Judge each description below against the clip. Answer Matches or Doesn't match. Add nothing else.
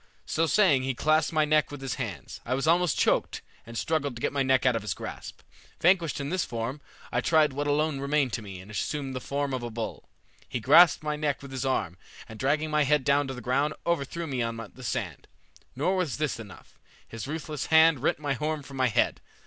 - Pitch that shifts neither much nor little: Matches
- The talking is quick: Matches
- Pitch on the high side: Doesn't match